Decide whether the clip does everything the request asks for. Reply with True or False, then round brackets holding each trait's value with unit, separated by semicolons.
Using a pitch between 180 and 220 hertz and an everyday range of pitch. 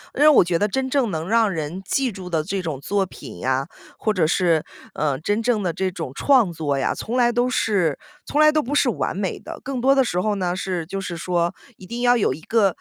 False (190 Hz; 6.2 semitones)